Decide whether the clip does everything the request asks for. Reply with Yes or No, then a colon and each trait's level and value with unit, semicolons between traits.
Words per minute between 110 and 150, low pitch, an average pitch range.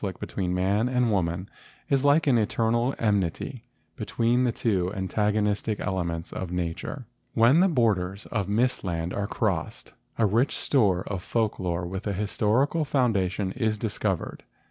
No: average, 160 wpm; low, 105 Hz; average, 4.1 semitones